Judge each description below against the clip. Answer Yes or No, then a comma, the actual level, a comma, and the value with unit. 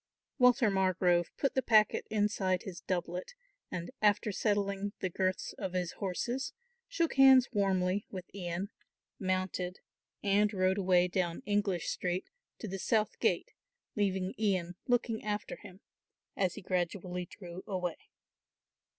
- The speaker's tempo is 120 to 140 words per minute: Yes, slow, 135 wpm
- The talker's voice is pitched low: No, high, 190 Hz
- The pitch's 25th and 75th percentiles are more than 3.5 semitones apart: No, narrow, 2.6 semitones